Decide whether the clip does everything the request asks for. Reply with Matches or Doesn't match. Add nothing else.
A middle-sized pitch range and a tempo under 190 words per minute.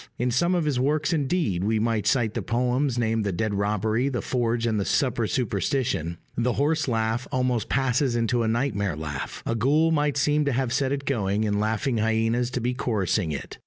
Doesn't match